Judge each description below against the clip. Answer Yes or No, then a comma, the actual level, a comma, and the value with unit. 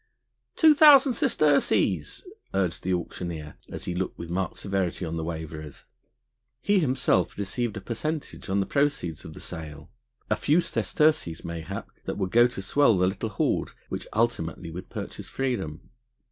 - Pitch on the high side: No, very low, 95 Hz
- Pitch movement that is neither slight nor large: No, wide, 8.2 semitones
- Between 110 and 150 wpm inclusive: No, average, 160 wpm